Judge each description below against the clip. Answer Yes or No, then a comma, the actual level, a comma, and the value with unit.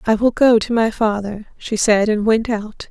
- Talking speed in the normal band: No, fast, 225 wpm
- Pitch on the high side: Yes, high, 220 Hz